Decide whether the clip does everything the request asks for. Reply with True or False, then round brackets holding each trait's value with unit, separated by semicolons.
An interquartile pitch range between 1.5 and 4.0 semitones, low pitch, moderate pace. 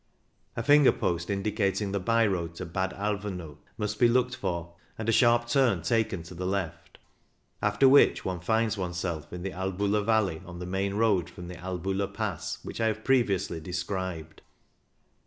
True (3.7 semitones; 95 Hz; 175 wpm)